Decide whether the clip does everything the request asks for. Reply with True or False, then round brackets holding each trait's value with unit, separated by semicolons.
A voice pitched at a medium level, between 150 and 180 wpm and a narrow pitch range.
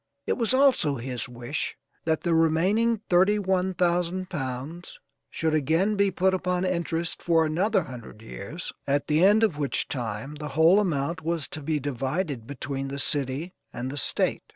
False (160 Hz; 170 wpm; 5.0 semitones)